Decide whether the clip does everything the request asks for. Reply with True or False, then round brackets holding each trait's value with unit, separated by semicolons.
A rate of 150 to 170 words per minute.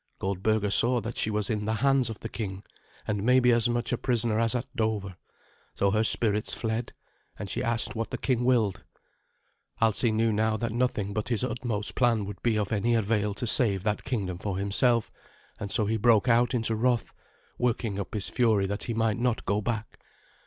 False (200 wpm)